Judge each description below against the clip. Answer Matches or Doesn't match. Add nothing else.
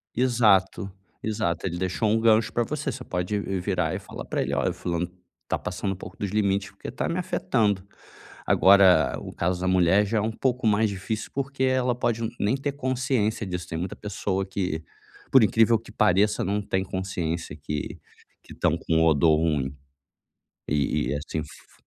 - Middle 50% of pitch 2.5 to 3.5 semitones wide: Doesn't match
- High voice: Doesn't match